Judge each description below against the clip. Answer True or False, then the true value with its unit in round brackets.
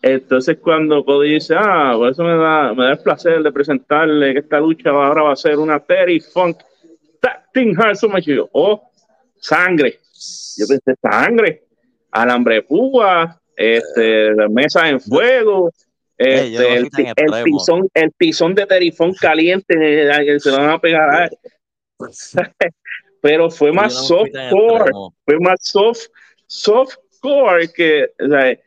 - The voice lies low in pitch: False (160 Hz)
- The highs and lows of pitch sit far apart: False (4.8 semitones)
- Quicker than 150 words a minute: False (140 wpm)